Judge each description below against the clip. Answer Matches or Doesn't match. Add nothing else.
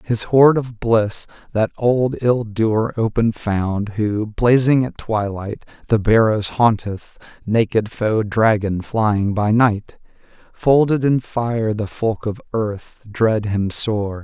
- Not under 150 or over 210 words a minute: Doesn't match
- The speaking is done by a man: Matches